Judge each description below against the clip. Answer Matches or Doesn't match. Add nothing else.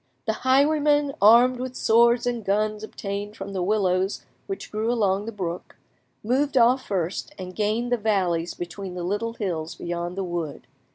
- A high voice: Matches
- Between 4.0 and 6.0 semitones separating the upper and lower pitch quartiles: Matches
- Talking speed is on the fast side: Doesn't match